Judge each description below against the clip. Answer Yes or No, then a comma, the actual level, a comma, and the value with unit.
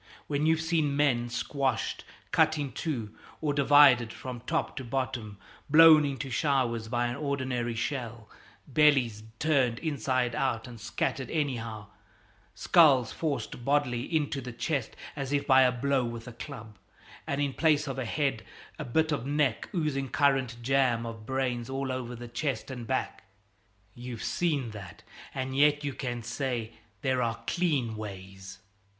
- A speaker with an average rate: Yes, average, 155 wpm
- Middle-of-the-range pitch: No, low, 130 Hz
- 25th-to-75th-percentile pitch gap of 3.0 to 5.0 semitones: Yes, average, 3.4 semitones